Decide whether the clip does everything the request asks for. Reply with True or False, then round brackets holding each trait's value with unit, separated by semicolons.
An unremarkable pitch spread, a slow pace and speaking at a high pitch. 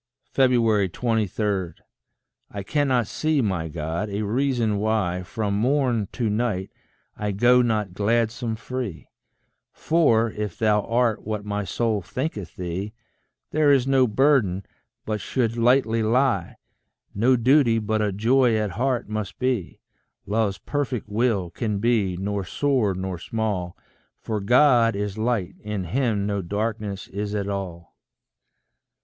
False (3.4 semitones; 130 wpm; 110 Hz)